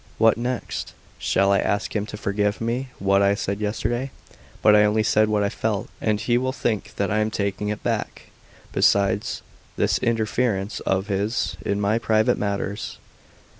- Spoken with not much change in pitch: Yes, narrow, 1.8 semitones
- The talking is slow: No, average, 170 wpm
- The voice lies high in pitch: No, low, 105 Hz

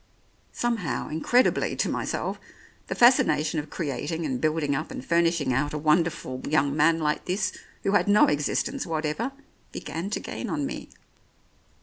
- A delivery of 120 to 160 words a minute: Yes, average, 155 wpm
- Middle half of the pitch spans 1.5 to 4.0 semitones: Yes, average, 3.5 semitones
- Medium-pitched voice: Yes, medium, 155 Hz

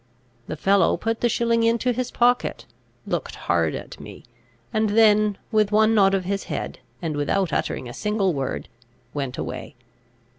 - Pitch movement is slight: No, average, 3.2 semitones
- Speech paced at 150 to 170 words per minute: Yes, average, 160 wpm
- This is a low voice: No, high, 210 Hz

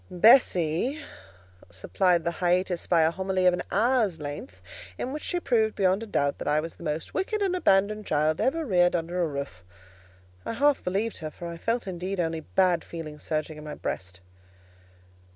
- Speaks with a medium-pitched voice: Yes, medium, 180 Hz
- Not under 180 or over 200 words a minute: Yes, average, 185 wpm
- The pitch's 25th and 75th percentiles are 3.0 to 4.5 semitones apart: No, average, 5.2 semitones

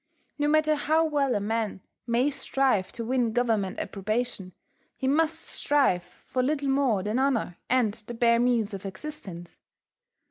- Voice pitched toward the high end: Yes, high, 240 Hz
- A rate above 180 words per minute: No, average, 150 wpm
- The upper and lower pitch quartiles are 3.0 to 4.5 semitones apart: No, average, 5.0 semitones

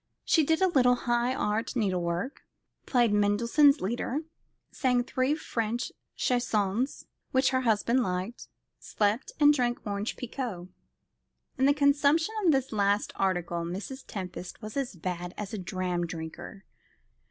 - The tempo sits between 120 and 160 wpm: Yes, average, 140 wpm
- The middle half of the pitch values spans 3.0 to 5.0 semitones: No, wide, 5.4 semitones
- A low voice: No, high, 230 Hz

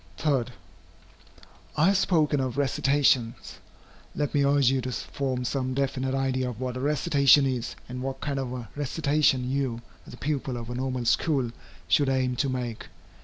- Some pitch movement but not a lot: No, narrow, 2.1 semitones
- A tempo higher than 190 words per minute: No, average, 170 wpm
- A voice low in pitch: Yes, low, 130 Hz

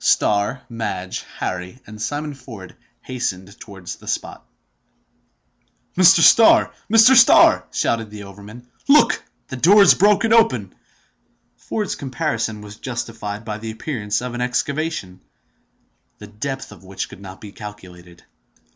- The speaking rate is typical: No, slow, 130 wpm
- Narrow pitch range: No, wide, 5.5 semitones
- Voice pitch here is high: No, low, 110 Hz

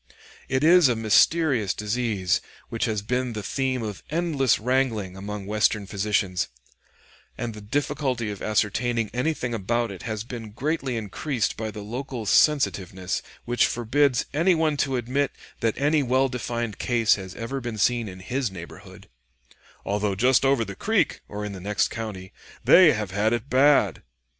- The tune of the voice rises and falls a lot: No, average, 4.1 semitones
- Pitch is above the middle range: No, low, 115 Hz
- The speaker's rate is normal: Yes, average, 160 wpm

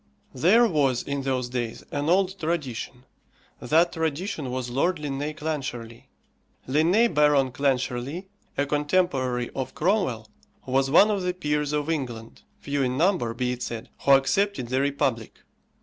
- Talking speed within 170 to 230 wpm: No, average, 145 wpm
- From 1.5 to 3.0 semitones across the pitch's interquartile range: No, average, 4.3 semitones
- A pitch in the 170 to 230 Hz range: No, medium, 140 Hz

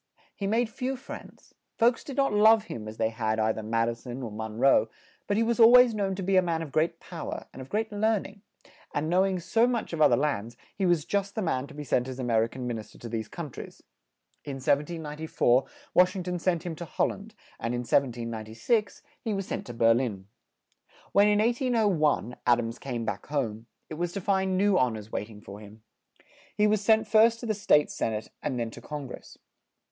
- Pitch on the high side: No, medium, 155 Hz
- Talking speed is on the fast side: Yes, fast, 240 wpm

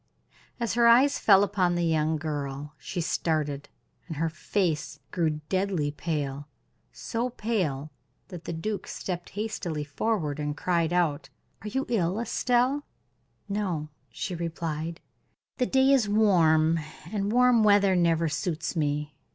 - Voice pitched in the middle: Yes, medium, 170 Hz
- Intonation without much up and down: No, average, 5.3 semitones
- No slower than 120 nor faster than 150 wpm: Yes, slow, 135 wpm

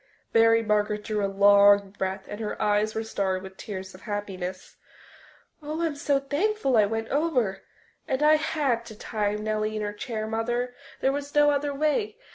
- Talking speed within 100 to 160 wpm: No, average, 180 wpm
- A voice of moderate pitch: No, high, 220 Hz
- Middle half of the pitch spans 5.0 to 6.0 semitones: Yes, average, 5.3 semitones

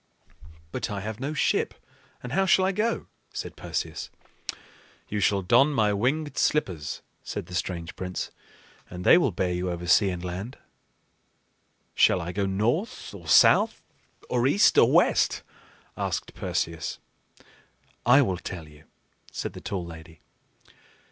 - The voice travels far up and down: Yes, wide, 6.7 semitones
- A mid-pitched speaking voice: No, low, 100 Hz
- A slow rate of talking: No, average, 145 wpm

